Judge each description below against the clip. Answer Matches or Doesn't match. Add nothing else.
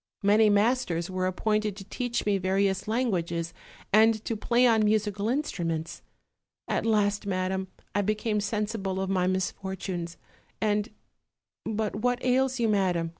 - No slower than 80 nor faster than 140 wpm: Matches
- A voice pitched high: Matches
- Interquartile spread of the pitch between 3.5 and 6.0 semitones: Doesn't match